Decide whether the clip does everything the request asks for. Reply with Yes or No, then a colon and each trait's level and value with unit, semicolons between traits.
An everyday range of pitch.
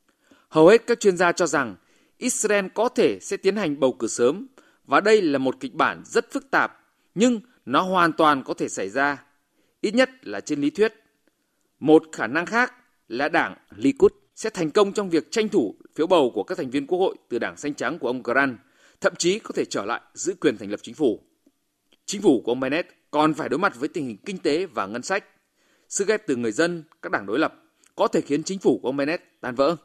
No: wide, 8.7 semitones